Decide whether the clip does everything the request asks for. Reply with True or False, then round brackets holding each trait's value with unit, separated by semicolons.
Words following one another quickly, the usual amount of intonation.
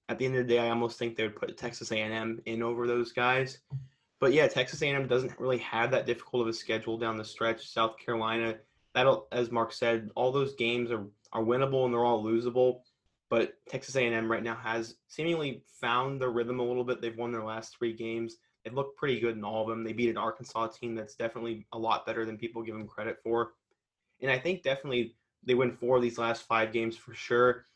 False (230 wpm; 1.7 semitones)